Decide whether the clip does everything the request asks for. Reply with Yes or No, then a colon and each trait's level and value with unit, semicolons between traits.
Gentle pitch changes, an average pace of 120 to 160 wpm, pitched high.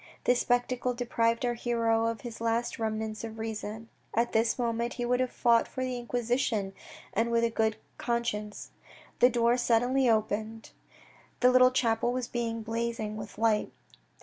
Yes: narrow, 1.5 semitones; average, 155 wpm; high, 230 Hz